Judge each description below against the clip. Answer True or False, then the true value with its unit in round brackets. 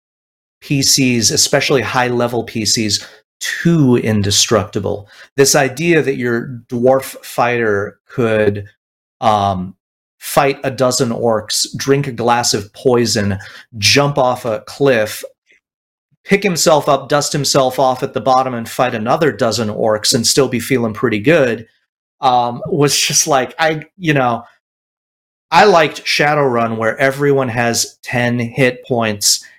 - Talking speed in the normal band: False (130 wpm)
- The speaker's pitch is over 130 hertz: False (125 Hz)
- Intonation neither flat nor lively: True (3.4 semitones)